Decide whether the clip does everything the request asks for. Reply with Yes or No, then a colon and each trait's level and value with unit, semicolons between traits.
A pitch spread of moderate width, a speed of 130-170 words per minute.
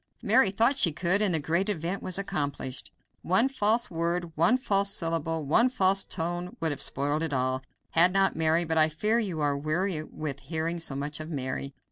No: average, 4.1 semitones; average, 195 wpm